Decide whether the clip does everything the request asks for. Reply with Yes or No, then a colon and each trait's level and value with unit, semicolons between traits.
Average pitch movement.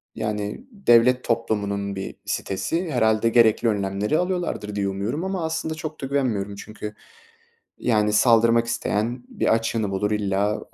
Yes: average, 3.5 semitones